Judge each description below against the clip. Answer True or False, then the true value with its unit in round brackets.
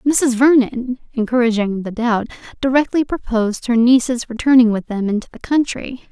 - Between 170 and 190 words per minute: False (145 wpm)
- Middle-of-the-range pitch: False (240 Hz)